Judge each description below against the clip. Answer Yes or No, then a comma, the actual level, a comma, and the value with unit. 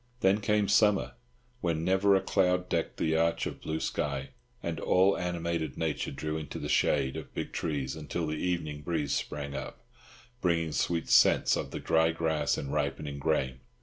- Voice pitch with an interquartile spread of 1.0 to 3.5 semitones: Yes, average, 3.2 semitones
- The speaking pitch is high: No, very low, 80 Hz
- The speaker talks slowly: No, average, 175 wpm